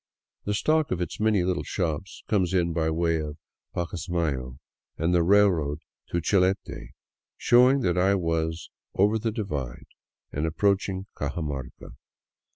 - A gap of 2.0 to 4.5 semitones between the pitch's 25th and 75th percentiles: Yes, average, 3.7 semitones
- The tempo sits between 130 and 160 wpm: Yes, average, 145 wpm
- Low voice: Yes, very low, 90 Hz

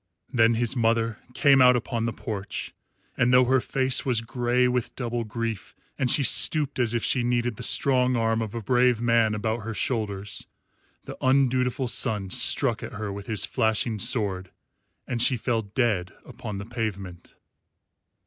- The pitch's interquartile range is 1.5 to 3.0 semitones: Yes, narrow, 2.5 semitones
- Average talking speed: Yes, average, 170 wpm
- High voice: No, low, 115 Hz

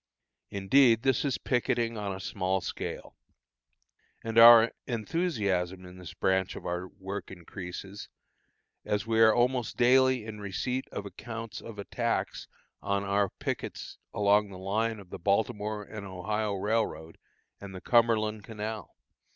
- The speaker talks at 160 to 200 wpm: No, average, 140 wpm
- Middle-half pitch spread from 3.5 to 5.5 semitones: No, average, 3.0 semitones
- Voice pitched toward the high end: No, low, 105 Hz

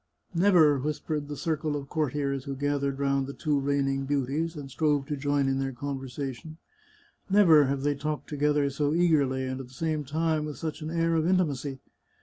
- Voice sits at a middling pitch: Yes, medium, 145 Hz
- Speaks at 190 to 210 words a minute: Yes, average, 195 wpm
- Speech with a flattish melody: Yes, narrow, 2.2 semitones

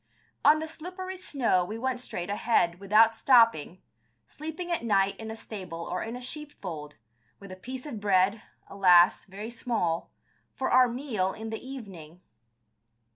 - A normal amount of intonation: No, wide, 5.7 semitones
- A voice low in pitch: No, high, 220 Hz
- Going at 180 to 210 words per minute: No, average, 155 wpm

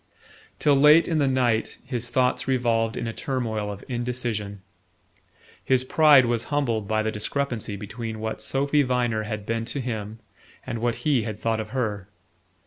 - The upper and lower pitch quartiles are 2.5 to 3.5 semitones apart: Yes, average, 3.1 semitones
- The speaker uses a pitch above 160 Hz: No, low, 120 Hz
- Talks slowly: No, average, 165 wpm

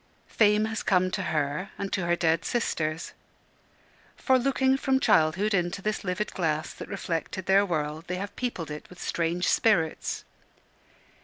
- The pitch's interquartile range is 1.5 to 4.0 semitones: No, average, 4.6 semitones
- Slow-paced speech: No, average, 155 wpm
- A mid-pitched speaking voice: Yes, medium, 180 Hz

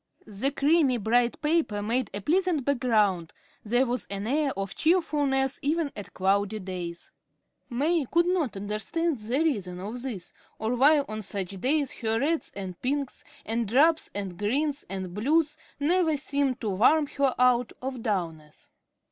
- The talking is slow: No, average, 155 wpm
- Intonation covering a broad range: Yes, wide, 6.2 semitones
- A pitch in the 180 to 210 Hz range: No, very high, 250 Hz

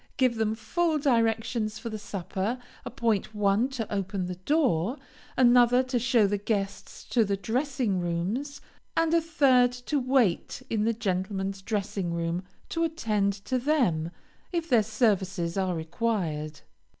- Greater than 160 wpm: No, average, 145 wpm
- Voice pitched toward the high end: Yes, high, 220 Hz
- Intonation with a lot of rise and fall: No, average, 4.7 semitones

